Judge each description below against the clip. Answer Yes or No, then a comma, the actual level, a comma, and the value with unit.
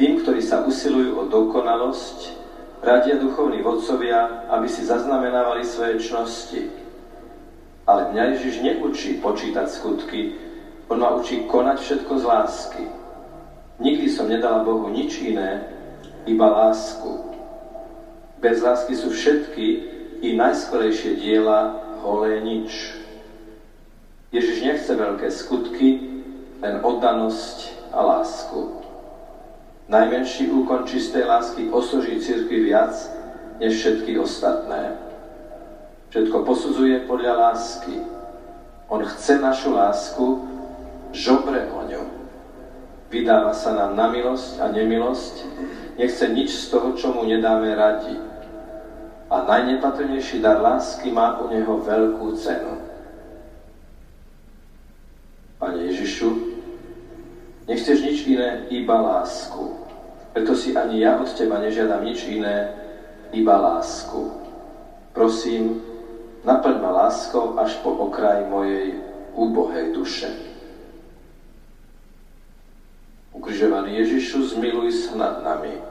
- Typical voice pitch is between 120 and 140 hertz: Yes, low, 135 Hz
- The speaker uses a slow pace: Yes, slow, 105 wpm